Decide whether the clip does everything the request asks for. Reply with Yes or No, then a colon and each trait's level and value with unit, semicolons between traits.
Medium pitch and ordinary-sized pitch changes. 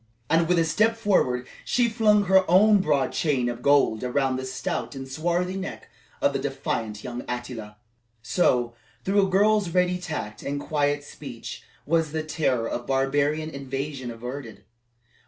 No: medium, 145 Hz; wide, 6.1 semitones